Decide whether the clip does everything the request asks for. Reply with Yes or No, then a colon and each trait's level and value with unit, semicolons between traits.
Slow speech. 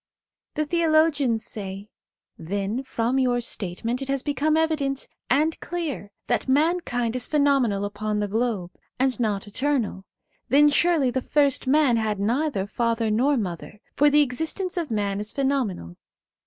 No: average, 155 wpm